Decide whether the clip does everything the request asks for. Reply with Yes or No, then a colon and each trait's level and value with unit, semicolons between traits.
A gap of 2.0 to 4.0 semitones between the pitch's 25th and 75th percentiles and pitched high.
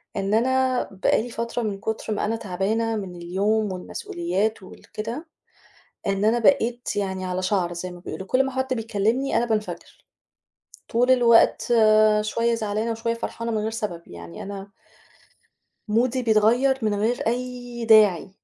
Yes: average, 3.2 semitones; high, 220 Hz